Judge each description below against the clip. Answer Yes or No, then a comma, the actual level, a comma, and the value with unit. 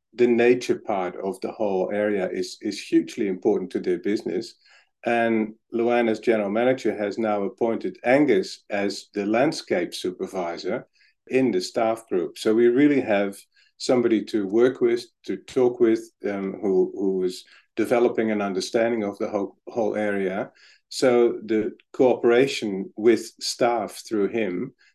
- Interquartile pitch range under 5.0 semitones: No, wide, 5.4 semitones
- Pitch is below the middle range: Yes, low, 115 Hz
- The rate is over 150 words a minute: No, average, 145 wpm